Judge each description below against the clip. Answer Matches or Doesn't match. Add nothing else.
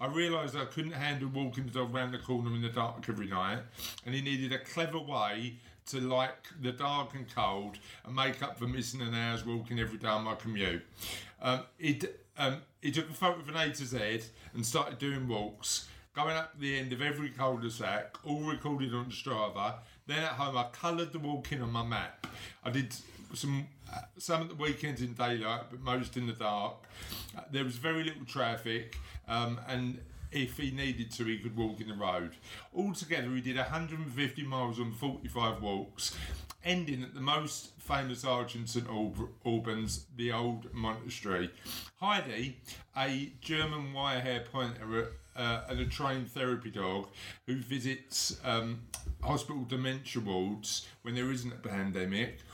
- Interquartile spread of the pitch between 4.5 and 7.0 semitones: Doesn't match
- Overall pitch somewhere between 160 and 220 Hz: Doesn't match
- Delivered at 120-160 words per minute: Doesn't match